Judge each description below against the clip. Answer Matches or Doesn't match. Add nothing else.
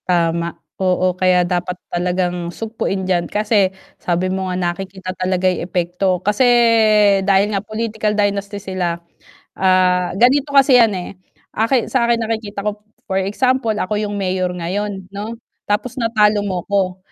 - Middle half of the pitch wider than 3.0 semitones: Doesn't match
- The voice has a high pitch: Matches